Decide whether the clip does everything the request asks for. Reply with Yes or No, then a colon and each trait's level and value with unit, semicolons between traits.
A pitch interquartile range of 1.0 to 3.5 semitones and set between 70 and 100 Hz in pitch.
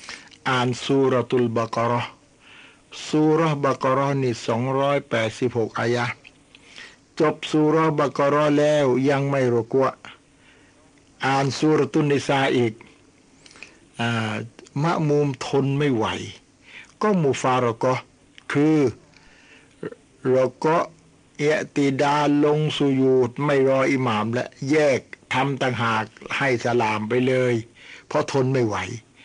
No: average, 3.2 semitones; low, 135 Hz